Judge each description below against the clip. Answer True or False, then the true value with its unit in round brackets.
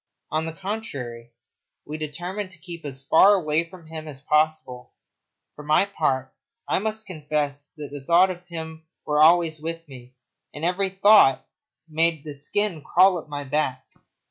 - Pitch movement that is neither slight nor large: True (3.3 semitones)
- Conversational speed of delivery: True (155 wpm)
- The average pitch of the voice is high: False (155 Hz)